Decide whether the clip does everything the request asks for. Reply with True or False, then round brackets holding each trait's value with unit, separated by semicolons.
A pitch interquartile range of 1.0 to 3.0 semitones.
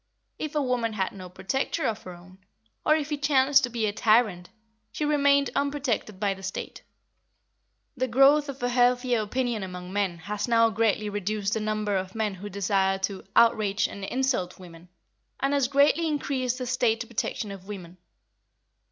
False (5.1 semitones)